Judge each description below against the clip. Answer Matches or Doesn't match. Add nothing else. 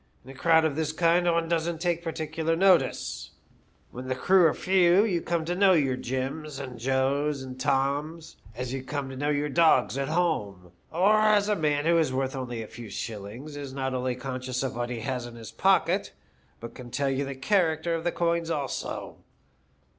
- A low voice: Doesn't match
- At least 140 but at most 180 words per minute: Doesn't match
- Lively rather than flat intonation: Doesn't match